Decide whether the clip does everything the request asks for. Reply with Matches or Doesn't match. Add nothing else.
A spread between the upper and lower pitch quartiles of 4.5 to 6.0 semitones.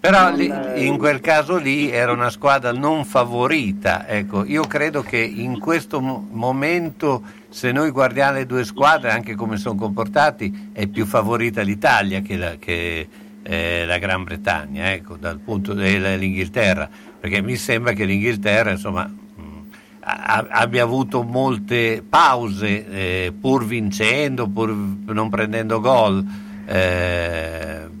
Doesn't match